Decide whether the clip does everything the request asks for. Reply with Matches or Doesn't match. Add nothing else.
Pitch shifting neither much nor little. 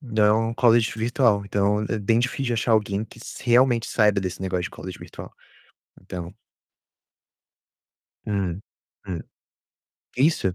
Matches